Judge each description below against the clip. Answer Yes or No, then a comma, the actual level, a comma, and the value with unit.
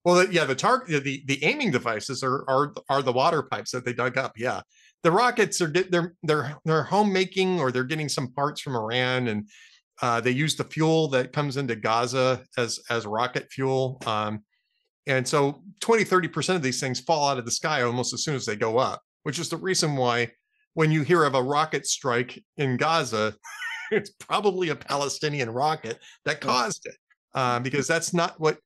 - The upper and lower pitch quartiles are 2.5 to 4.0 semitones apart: No, average, 4.8 semitones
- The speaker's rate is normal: Yes, average, 195 wpm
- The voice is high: No, medium, 140 Hz